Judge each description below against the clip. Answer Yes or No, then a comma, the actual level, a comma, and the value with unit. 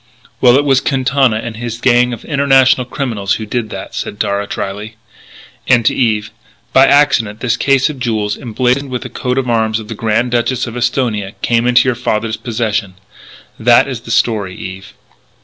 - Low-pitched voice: Yes, low, 120 Hz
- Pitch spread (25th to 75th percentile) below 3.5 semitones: Yes, average, 2.9 semitones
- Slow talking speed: No, average, 185 wpm